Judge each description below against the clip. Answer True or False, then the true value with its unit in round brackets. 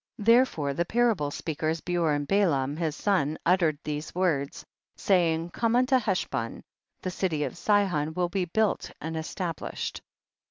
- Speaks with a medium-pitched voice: True (170 Hz)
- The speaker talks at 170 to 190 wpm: False (155 wpm)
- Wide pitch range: False (4.5 semitones)